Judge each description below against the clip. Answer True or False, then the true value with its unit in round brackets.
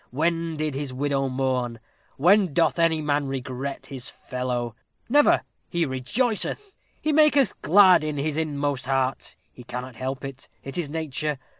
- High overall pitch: False (145 Hz)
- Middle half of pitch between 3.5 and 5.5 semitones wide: True (4.1 semitones)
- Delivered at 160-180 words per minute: False (150 wpm)